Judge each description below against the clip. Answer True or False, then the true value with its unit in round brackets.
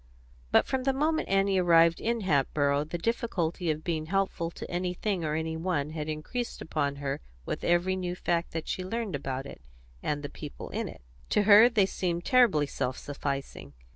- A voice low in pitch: False (170 Hz)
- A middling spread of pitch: True (4.5 semitones)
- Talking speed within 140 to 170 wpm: False (190 wpm)